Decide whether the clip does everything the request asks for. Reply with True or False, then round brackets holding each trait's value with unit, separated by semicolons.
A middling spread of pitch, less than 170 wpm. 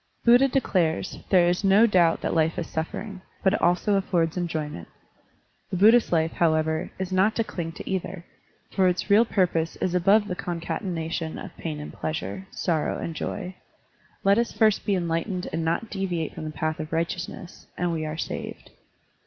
False (3.1 semitones; 175 wpm)